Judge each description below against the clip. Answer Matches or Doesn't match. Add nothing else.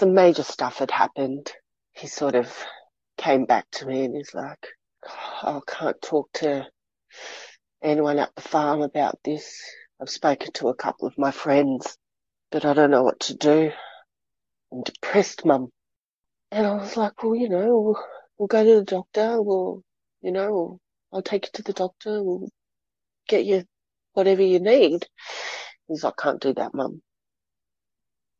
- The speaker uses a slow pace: Doesn't match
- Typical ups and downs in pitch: Doesn't match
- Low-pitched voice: Doesn't match